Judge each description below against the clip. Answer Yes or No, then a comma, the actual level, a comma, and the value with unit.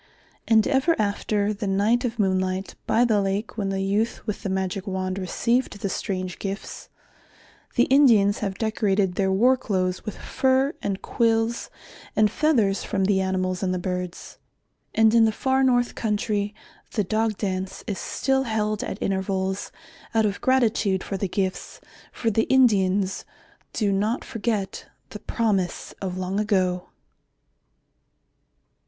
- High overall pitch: Yes, high, 205 Hz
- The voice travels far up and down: No, average, 2.9 semitones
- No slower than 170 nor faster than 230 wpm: No, average, 150 wpm